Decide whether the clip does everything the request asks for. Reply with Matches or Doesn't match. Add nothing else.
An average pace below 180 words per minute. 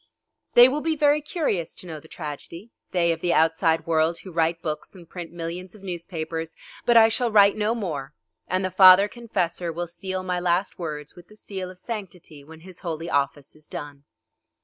Doesn't match